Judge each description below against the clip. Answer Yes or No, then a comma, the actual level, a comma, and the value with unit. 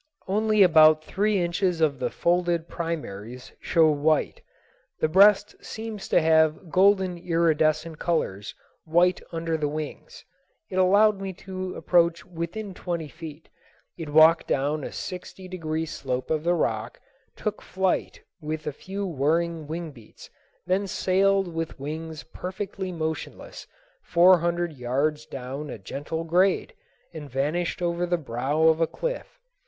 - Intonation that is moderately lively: Yes, average, 3.1 semitones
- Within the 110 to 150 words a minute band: Yes, average, 140 wpm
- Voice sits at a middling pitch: Yes, medium, 165 Hz